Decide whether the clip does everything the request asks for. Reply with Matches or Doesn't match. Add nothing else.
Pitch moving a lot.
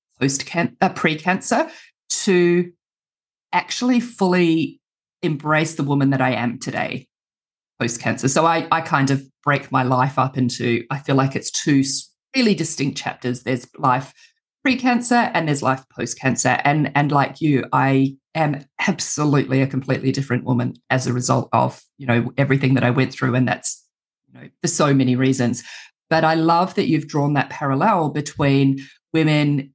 Doesn't match